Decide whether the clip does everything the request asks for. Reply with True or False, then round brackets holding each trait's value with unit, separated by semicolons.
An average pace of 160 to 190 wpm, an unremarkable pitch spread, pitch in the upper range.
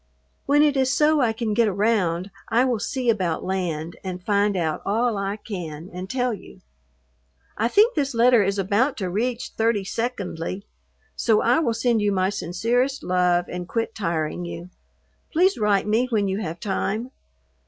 True (175 wpm; 4.8 semitones; 210 Hz)